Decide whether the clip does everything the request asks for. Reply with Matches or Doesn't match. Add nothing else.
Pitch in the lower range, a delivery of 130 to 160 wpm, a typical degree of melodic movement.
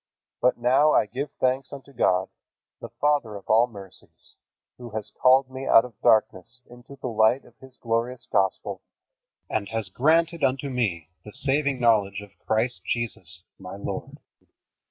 Matches